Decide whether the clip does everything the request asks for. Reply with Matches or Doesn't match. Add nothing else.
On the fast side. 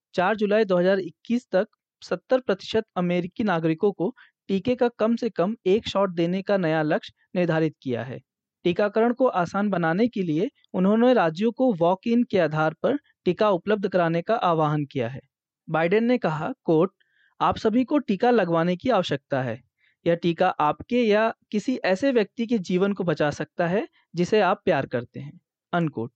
Doesn't match